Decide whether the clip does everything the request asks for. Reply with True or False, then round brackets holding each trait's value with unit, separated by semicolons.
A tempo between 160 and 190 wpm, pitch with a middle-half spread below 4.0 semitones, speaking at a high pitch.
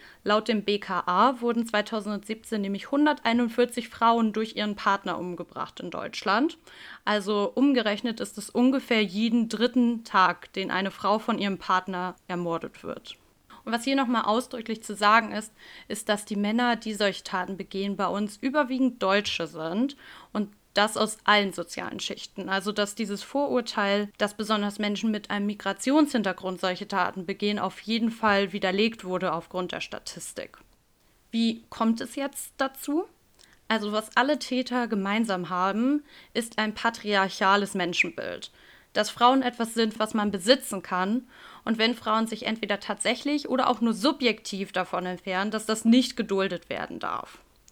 False (150 wpm; 3.2 semitones; 215 Hz)